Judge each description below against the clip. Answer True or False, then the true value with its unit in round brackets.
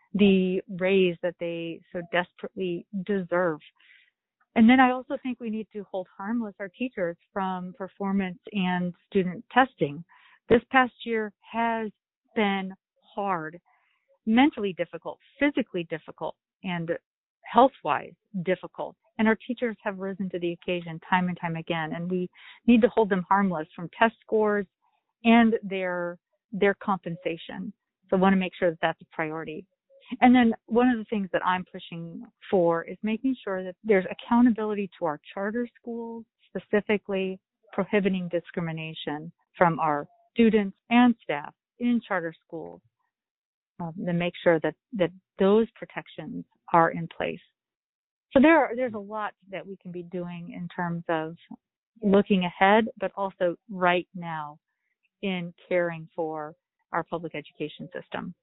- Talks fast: False (145 wpm)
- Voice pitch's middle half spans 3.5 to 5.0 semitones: True (4.3 semitones)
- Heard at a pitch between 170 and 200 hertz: True (190 Hz)